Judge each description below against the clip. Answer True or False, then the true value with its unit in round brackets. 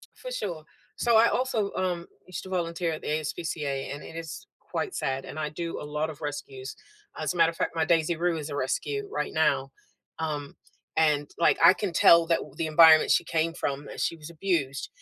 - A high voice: False (165 Hz)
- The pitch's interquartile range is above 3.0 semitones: False (2.6 semitones)